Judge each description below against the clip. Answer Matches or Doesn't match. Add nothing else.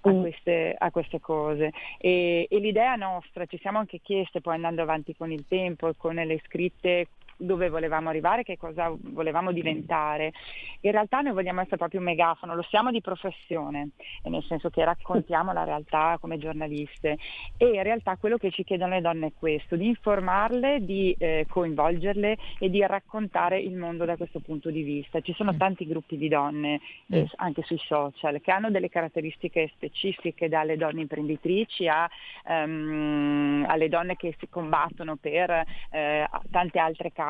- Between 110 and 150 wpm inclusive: Doesn't match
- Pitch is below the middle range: Doesn't match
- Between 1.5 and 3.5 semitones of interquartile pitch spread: Matches